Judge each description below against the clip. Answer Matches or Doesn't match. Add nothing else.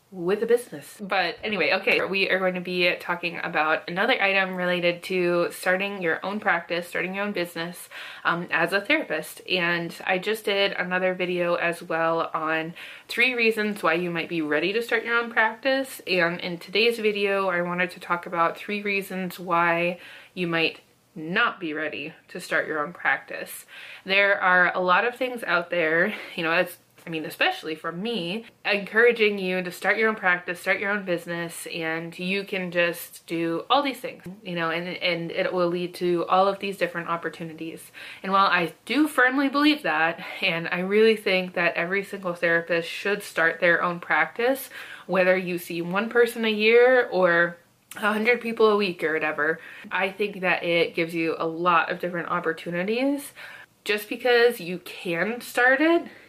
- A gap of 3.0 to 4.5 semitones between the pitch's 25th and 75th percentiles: Matches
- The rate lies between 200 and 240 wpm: Doesn't match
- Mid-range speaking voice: Matches